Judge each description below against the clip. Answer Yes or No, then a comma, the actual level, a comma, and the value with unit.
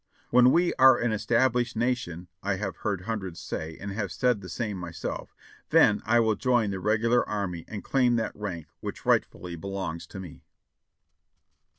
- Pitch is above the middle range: No, low, 105 Hz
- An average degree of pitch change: Yes, average, 4.5 semitones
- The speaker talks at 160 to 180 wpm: Yes, average, 175 wpm